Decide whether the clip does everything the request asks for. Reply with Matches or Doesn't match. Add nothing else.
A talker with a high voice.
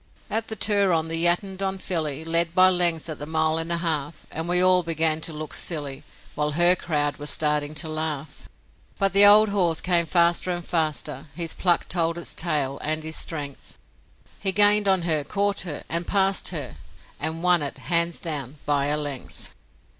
Doesn't match